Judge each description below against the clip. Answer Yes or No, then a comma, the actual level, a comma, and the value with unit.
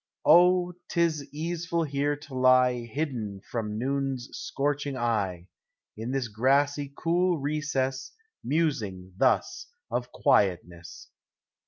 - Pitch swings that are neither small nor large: Yes, average, 4.3 semitones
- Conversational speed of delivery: No, slow, 110 wpm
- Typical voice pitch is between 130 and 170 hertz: Yes, low, 135 Hz